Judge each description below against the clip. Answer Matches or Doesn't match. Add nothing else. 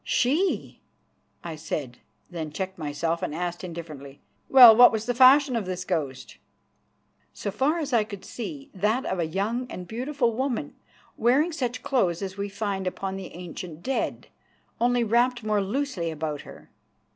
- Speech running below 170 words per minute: Matches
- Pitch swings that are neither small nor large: Doesn't match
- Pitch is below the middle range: Doesn't match